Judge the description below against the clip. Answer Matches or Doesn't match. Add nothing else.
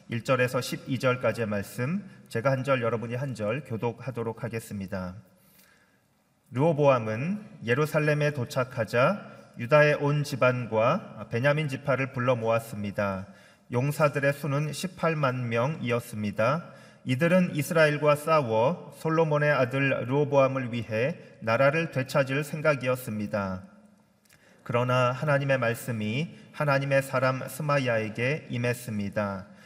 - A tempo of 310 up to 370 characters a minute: Doesn't match